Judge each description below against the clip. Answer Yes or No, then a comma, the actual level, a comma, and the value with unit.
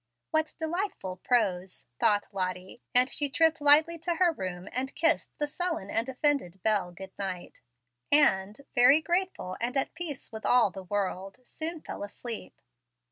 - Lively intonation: Yes, wide, 8.5 semitones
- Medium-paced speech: Yes, average, 155 wpm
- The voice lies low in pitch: No, very high, 250 Hz